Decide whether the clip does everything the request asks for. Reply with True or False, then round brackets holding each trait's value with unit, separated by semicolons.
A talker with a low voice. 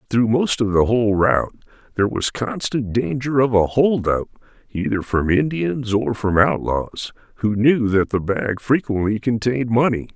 True (115 Hz)